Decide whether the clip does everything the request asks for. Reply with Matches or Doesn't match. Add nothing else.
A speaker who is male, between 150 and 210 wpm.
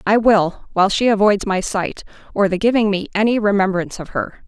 Doesn't match